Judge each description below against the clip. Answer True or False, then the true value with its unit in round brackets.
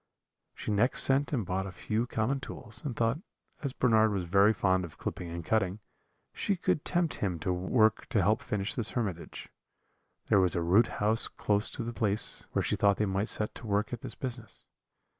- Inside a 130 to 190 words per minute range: False (200 wpm)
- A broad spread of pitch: False (3.6 semitones)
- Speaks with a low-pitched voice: True (105 Hz)